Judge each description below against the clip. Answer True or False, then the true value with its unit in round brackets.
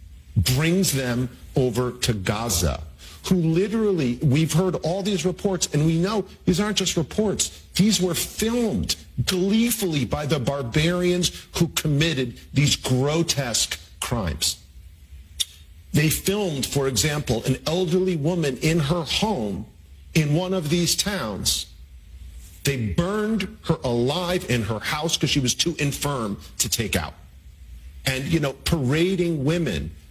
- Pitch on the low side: False (145 Hz)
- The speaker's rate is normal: False (130 wpm)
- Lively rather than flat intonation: True (8.1 semitones)